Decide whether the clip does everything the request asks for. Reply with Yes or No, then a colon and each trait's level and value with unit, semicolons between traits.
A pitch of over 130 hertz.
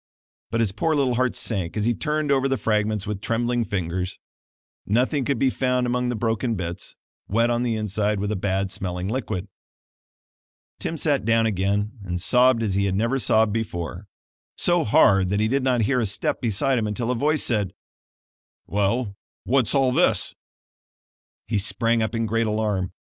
No: low, 115 Hz